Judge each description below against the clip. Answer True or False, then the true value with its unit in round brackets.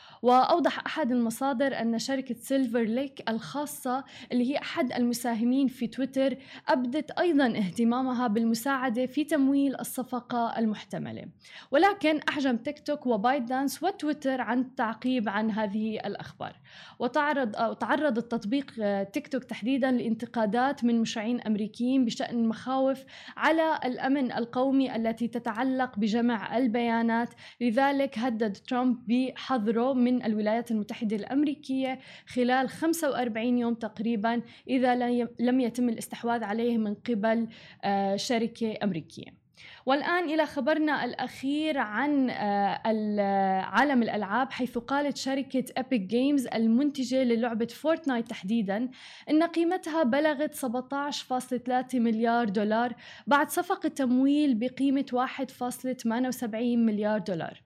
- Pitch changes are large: False (2.8 semitones)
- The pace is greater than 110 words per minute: False (105 wpm)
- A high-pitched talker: True (250 Hz)